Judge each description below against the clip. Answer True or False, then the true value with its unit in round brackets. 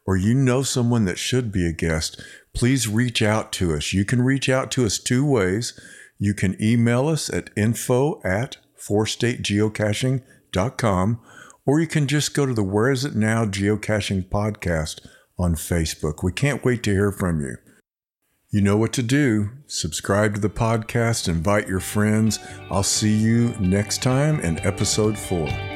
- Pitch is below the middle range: True (110 Hz)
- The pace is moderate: True (170 wpm)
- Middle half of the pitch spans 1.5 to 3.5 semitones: False (4.1 semitones)